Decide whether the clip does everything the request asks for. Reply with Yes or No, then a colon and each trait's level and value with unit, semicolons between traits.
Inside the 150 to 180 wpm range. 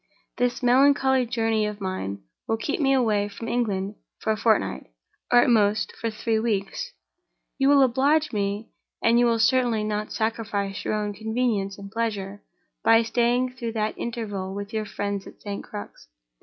Yes: average, 160 wpm